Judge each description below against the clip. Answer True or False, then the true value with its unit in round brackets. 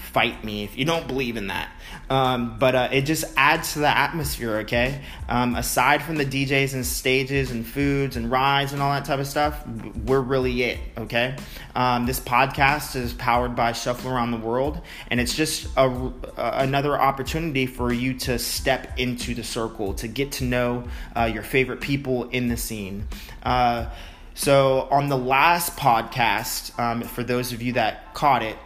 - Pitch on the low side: True (125 Hz)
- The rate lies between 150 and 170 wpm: False (185 wpm)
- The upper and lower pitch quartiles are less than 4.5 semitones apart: True (2.4 semitones)